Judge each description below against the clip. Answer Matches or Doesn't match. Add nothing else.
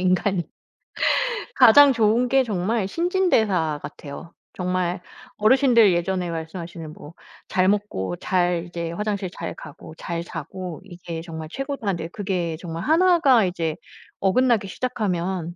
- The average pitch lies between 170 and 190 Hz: Matches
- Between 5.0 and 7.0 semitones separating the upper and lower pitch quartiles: Doesn't match